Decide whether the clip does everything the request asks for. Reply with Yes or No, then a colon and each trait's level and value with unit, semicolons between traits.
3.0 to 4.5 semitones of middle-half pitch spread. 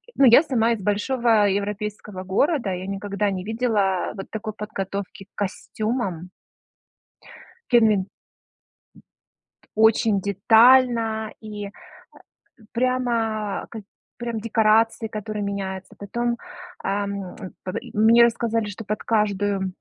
No: narrow, 2.4 semitones